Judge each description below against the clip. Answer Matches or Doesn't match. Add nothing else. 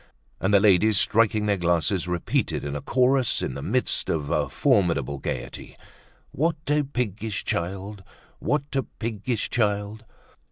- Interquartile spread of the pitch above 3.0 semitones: Matches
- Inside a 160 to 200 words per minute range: Doesn't match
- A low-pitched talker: Matches